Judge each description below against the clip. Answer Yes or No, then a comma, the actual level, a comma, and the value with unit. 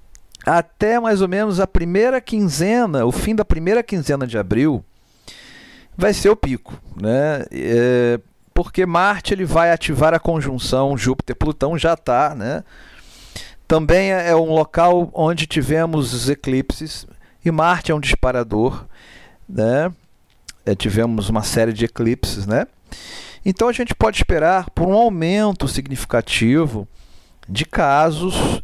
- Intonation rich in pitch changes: Yes, wide, 6.8 semitones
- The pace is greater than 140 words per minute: No, average, 135 wpm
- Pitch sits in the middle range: Yes, medium, 160 Hz